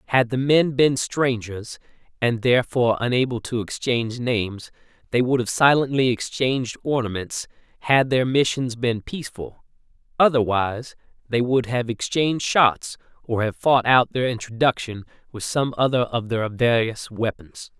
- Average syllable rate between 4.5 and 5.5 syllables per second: Yes, 4.7 syllables/s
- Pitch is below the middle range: Yes, low, 120 Hz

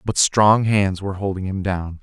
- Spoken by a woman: No, male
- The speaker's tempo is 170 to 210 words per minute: Yes, fast, 205 wpm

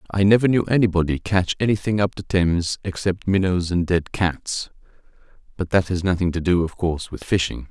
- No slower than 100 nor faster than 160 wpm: No, average, 185 wpm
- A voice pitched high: No, very low, 90 Hz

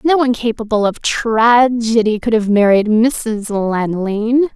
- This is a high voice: Yes, high, 225 Hz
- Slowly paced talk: Yes, slow, 130 wpm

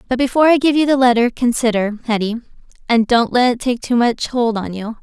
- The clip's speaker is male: No, female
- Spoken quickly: Yes, fast, 225 wpm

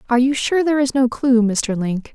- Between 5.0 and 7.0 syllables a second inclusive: Yes, 5.6 syllables/s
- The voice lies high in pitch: Yes, very high, 250 Hz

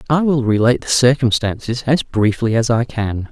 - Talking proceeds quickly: No, average, 180 wpm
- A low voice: Yes, low, 120 Hz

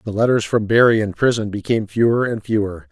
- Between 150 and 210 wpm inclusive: Yes, fast, 205 wpm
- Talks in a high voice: No, low, 110 Hz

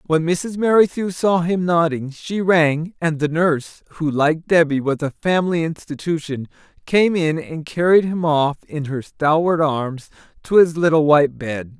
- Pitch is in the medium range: Yes, medium, 160 Hz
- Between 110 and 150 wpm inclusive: No, average, 160 wpm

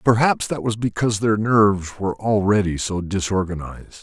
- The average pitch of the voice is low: Yes, low, 105 Hz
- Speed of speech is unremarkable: Yes, average, 150 wpm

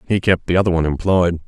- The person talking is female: No, male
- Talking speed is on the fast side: Yes, fast, 245 wpm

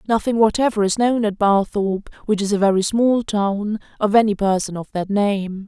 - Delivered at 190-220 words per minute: No, average, 170 wpm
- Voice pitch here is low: No, high, 205 Hz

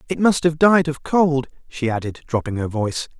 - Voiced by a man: Yes, male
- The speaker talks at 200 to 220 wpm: Yes, fast, 205 wpm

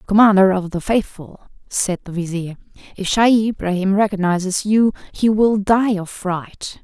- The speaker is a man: No, female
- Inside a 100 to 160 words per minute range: Yes, average, 150 wpm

